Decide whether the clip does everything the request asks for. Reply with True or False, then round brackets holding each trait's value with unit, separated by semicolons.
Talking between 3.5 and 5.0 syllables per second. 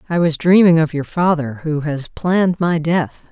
True (4.7 syllables/s)